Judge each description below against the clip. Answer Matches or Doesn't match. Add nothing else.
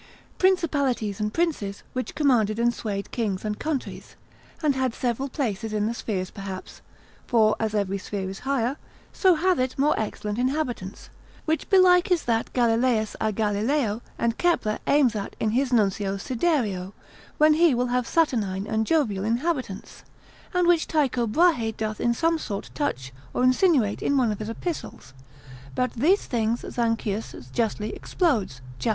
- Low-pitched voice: Doesn't match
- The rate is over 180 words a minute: Doesn't match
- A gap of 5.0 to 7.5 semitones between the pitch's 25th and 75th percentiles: Matches